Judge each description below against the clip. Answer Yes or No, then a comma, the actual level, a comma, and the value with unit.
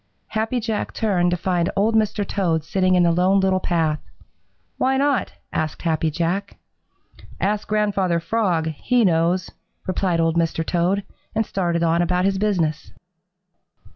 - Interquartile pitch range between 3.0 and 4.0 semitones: Yes, average, 3.4 semitones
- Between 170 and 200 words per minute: No, average, 145 wpm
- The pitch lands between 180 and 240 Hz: Yes, medium, 185 Hz